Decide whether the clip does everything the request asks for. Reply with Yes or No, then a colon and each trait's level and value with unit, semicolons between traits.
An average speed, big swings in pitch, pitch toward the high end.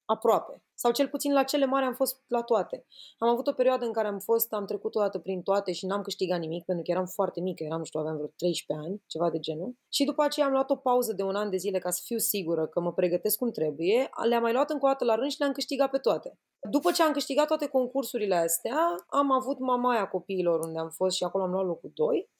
No: fast, 260 wpm; wide, 6.8 semitones; high, 220 Hz